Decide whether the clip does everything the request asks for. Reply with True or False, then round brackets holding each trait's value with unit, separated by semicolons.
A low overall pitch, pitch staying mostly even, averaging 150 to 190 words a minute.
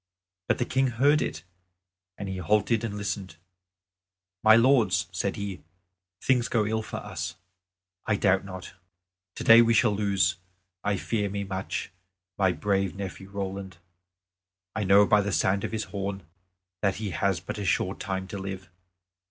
True (100 Hz; 2.1 semitones; 160 wpm)